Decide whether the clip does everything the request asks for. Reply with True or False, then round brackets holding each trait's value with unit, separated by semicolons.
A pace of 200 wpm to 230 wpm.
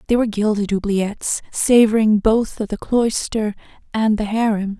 False (150 wpm)